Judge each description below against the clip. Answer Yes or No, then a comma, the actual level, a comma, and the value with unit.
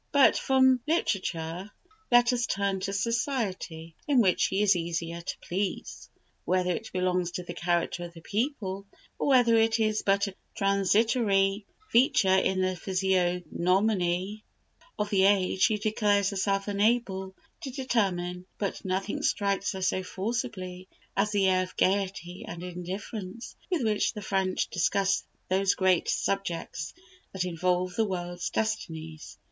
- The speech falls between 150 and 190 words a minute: No, average, 140 wpm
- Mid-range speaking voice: No, high, 195 Hz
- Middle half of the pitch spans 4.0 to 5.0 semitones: No, average, 2.7 semitones